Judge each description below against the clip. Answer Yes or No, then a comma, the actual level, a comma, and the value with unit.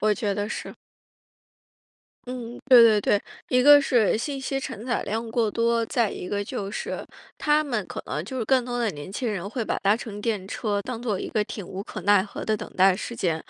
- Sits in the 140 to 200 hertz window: No, high, 220 Hz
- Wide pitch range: No, average, 3.2 semitones